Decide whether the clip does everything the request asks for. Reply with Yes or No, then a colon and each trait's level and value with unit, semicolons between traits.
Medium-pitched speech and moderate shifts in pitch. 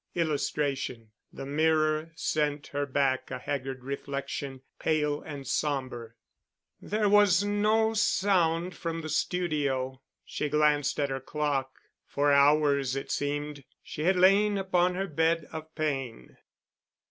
Yes: medium, 150 Hz; average, 3.4 semitones